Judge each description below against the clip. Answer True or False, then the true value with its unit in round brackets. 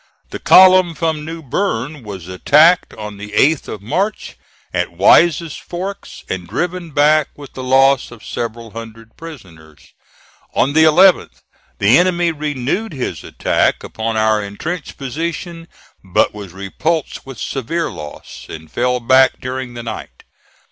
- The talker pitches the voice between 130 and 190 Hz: True (135 Hz)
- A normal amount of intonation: False (7.0 semitones)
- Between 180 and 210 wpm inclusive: False (140 wpm)